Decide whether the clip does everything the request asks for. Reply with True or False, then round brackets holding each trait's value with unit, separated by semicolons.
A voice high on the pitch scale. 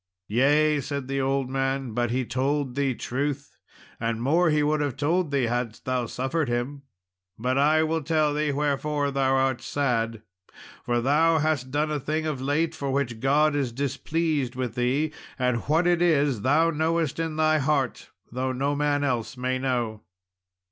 False (140 Hz)